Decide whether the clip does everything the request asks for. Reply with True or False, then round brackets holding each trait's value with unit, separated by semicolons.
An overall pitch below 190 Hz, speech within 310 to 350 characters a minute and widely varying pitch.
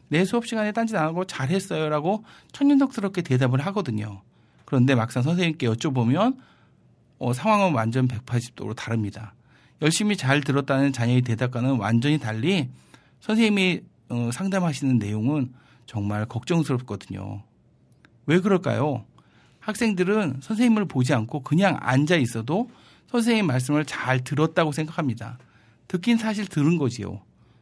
True (140 Hz; 315 characters per minute; 7.4 semitones)